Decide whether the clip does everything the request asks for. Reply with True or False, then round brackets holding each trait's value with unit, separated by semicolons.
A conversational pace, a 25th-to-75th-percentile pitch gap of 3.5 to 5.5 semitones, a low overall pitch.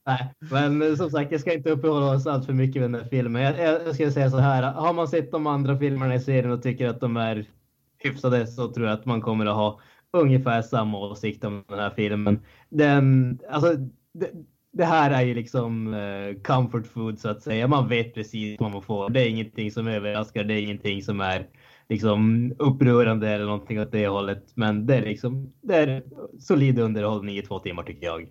False (210 wpm; 4.2 semitones; 120 Hz)